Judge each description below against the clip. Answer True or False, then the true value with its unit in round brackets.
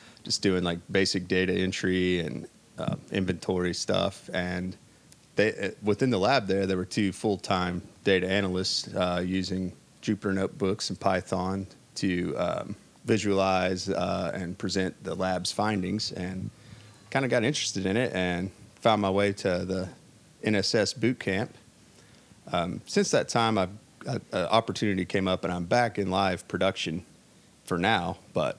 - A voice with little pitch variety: True (2.1 semitones)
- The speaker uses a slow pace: False (150 wpm)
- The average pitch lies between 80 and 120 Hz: True (95 Hz)